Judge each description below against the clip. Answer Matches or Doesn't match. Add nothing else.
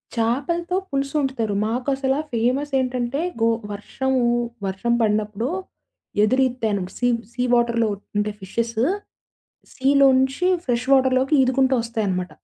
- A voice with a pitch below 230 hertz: Doesn't match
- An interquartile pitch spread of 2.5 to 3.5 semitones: Matches